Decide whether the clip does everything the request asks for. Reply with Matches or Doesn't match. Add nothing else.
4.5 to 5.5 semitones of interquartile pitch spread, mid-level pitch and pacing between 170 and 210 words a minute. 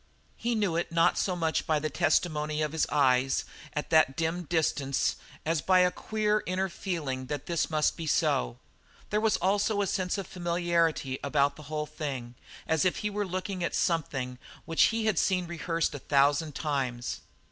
Doesn't match